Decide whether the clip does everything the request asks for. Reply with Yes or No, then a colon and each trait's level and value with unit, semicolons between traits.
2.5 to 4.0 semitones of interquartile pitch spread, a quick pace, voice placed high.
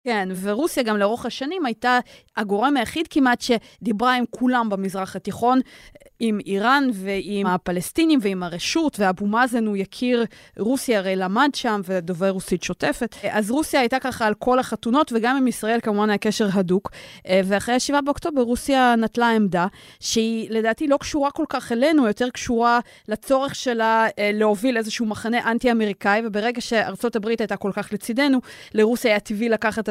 Yes: average, 3.6 semitones; fast, 155 wpm; high, 225 Hz